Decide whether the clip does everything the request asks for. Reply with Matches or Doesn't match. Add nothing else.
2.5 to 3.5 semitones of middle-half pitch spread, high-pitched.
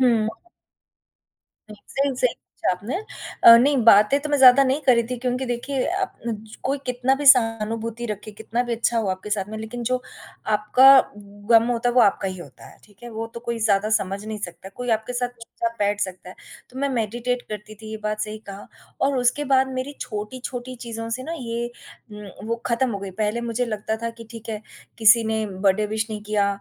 Matches